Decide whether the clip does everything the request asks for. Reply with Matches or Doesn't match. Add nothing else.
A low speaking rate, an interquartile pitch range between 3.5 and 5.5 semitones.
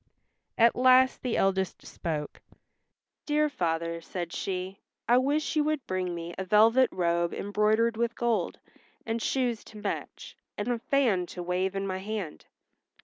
Doesn't match